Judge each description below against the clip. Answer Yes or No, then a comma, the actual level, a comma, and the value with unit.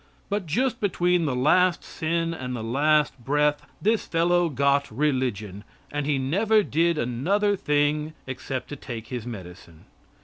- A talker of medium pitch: Yes, medium, 145 Hz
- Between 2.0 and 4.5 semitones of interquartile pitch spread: No, average, 5.1 semitones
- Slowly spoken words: No, average, 145 wpm